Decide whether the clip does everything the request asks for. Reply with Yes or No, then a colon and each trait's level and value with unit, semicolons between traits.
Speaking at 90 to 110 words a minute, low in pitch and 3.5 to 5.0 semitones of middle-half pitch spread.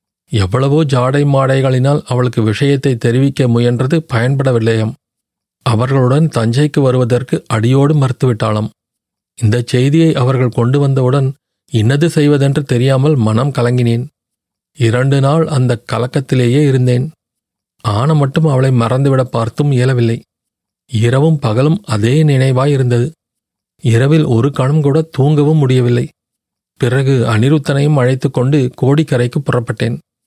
No: average, 100 wpm; low, 130 Hz; average, 2.9 semitones